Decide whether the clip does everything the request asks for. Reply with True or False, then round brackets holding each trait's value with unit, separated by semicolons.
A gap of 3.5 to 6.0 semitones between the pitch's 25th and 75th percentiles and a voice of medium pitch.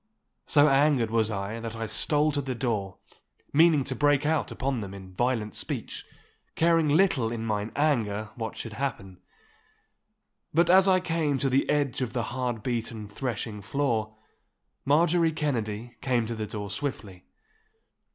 False (5.2 semitones; 120 Hz)